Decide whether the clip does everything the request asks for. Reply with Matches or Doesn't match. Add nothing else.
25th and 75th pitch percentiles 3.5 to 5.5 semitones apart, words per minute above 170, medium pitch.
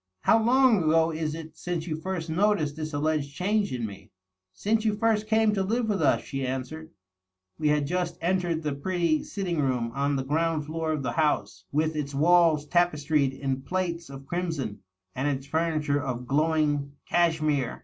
Matches